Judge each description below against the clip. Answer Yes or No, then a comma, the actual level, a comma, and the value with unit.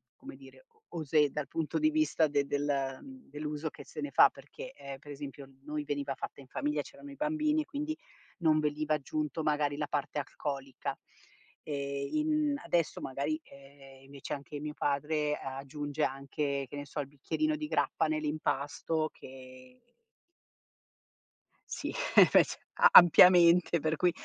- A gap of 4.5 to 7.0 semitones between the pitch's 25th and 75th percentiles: No, average, 2.8 semitones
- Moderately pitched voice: Yes, medium, 150 Hz